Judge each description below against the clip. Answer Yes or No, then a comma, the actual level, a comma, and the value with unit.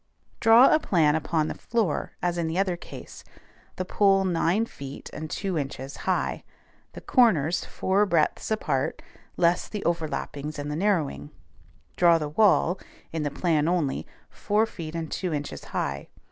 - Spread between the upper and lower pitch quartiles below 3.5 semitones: No, average, 4.3 semitones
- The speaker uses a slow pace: No, average, 160 wpm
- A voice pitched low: No, medium, 170 Hz